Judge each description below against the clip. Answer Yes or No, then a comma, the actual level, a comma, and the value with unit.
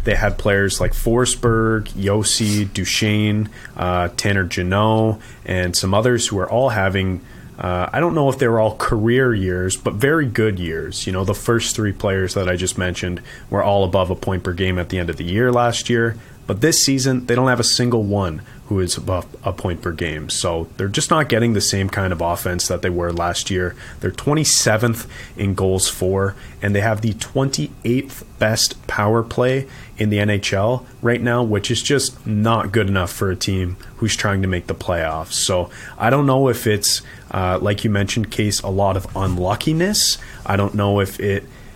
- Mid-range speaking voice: No, low, 105 Hz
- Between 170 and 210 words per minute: Yes, average, 200 wpm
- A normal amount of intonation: Yes, average, 4.1 semitones